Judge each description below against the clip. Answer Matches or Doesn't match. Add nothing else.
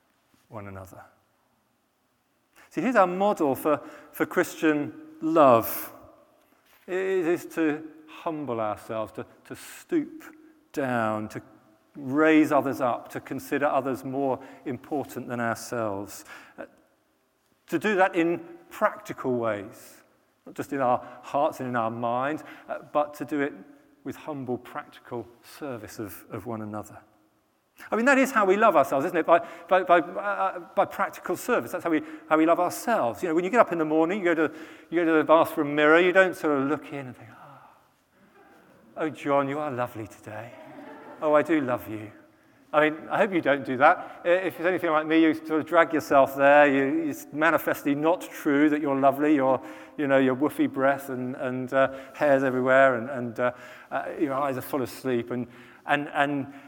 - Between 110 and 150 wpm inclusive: Doesn't match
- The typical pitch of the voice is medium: Matches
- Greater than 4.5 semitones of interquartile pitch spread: Matches